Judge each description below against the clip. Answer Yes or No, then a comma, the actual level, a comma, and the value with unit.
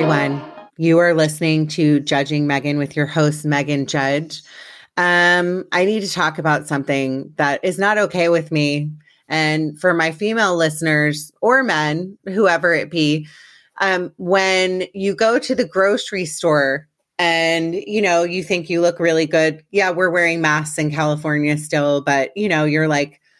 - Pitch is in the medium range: Yes, medium, 160 Hz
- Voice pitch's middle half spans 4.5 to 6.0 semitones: No, average, 3.4 semitones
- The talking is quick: No, average, 165 wpm